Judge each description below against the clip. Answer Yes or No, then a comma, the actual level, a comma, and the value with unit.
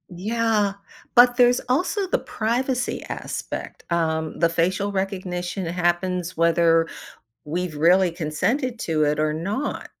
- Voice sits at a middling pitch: Yes, medium, 180 Hz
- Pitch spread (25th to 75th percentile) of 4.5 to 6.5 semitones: Yes, wide, 5.5 semitones